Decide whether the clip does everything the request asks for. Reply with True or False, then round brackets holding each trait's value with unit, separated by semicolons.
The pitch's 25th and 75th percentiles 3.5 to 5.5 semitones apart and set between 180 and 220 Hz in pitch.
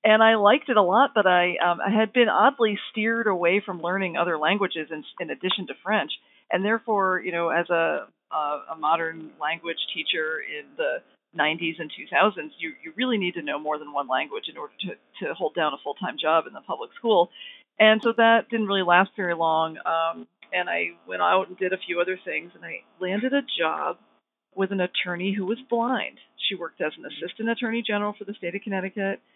True (4.7 semitones; 190 Hz)